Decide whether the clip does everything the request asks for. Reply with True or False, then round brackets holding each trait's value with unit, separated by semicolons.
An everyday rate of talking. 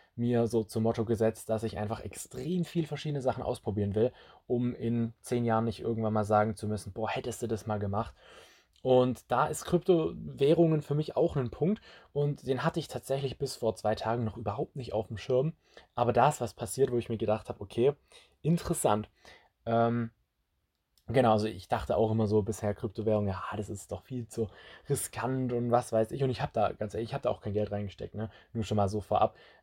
False (215 wpm)